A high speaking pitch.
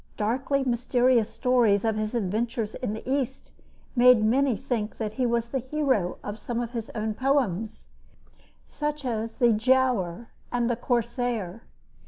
Yes: high, 235 Hz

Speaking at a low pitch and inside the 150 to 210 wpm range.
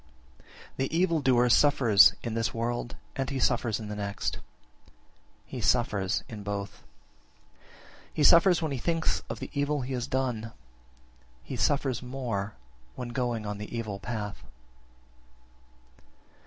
No: low, 120 Hz; average, 140 wpm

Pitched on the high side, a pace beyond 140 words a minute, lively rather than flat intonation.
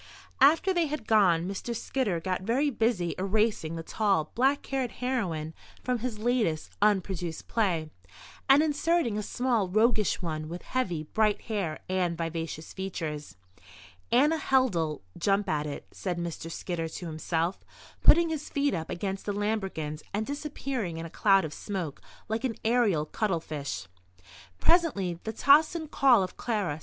Yes: high, 200 Hz; average, 150 wpm; wide, 6.9 semitones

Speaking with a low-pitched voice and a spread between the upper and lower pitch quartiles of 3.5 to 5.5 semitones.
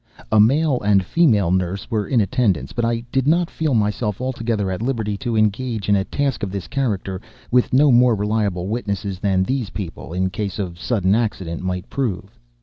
Yes: low, 105 Hz; average, 4.4 semitones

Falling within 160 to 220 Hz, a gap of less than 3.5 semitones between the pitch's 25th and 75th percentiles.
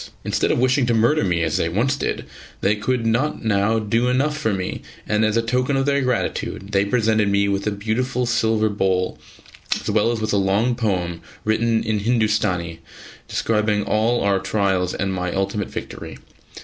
No: low, 110 Hz; average, 3.1 semitones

